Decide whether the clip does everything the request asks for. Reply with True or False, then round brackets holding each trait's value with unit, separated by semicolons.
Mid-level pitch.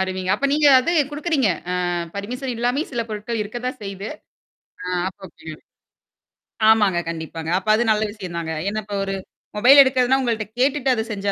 False (215 Hz)